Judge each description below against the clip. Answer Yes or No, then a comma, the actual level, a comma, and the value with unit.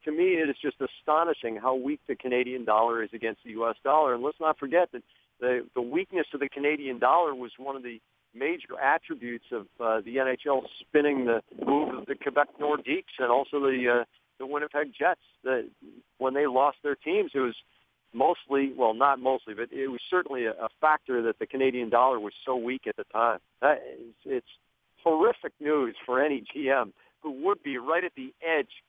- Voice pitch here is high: No, low, 135 Hz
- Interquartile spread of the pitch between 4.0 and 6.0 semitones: No, average, 3.5 semitones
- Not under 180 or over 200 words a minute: Yes, average, 195 wpm